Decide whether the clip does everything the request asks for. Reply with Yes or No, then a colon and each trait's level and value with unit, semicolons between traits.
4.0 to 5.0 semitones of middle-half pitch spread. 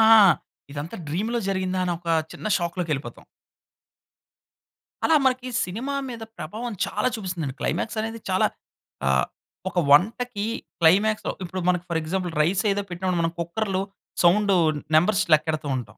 Yes: average, 4.4 semitones